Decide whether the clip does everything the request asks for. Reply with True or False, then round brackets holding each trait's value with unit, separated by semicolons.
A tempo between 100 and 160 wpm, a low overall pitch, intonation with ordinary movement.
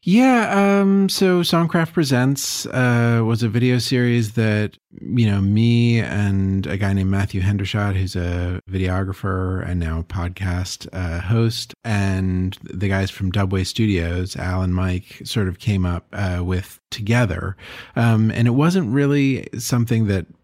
True (155 wpm; 100 Hz; 4.6 semitones)